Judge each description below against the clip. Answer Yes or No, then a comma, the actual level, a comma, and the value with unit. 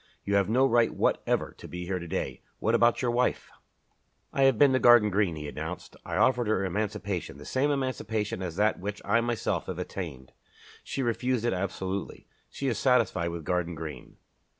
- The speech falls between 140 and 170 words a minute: No, average, 190 wpm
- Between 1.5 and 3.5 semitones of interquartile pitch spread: No, average, 5.1 semitones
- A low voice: Yes, low, 105 Hz